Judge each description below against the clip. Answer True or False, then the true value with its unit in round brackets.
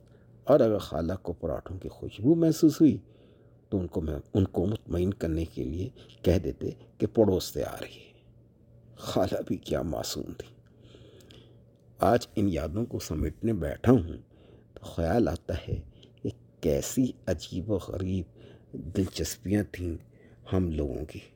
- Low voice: True (95 Hz)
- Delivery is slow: False (150 wpm)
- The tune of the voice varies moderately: True (4.8 semitones)